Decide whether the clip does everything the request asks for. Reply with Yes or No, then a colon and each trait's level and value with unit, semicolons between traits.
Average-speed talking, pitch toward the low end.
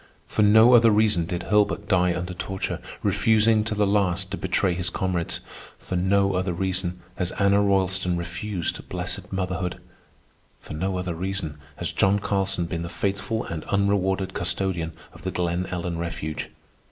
Yes: average, 160 wpm; very low, 95 Hz